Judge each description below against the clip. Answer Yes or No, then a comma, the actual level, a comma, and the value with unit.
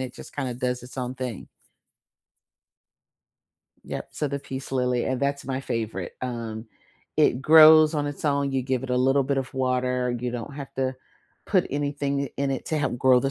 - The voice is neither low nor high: No, low, 130 Hz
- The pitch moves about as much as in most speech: No, narrow, 2.0 semitones